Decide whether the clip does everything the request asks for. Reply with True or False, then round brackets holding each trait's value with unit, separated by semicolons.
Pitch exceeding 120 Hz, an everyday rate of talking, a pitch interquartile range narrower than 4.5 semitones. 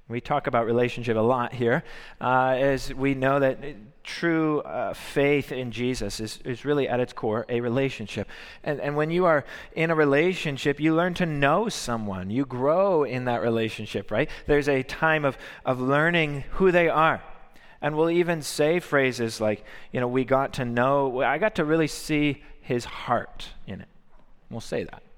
True (140 Hz; 185 wpm; 3.7 semitones)